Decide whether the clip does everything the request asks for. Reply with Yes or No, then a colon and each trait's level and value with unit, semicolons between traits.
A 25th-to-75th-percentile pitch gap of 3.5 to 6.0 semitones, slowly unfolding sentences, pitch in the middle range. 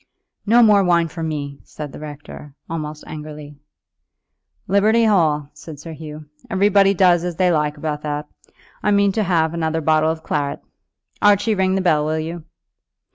No: average, 4.0 semitones; average, 165 wpm; medium, 160 Hz